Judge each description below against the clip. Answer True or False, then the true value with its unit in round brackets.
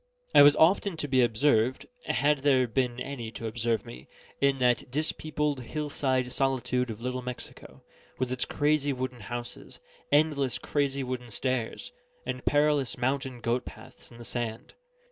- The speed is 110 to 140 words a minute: False (160 wpm)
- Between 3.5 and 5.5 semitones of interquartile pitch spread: False (2.9 semitones)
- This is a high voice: False (130 Hz)